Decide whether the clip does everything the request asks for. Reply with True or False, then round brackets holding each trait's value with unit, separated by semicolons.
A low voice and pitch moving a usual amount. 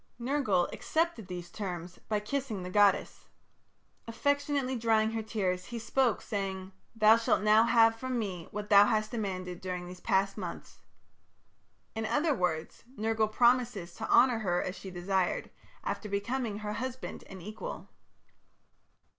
False (215 Hz; 3.8 semitones)